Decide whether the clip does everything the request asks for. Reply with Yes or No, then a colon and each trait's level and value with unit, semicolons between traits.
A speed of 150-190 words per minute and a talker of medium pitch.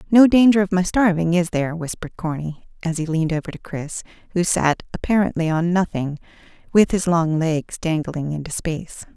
Yes: average, 175 wpm; medium, 170 Hz